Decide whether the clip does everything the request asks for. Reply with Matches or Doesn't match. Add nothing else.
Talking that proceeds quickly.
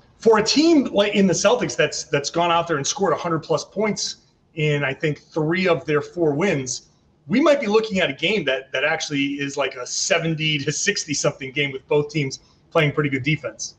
Matches